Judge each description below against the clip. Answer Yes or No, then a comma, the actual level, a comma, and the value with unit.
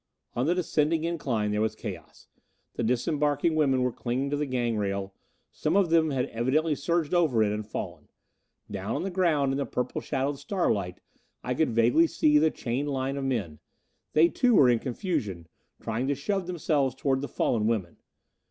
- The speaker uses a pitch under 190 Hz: Yes, low, 135 Hz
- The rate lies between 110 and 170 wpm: No, average, 185 wpm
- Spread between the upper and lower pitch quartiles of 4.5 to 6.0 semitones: Yes, average, 5.2 semitones